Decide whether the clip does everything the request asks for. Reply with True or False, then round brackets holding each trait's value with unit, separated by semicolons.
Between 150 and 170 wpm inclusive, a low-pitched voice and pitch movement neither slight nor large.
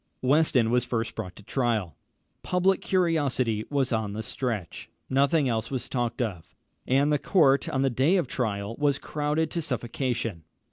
True (160 wpm; 130 Hz; 4.4 semitones)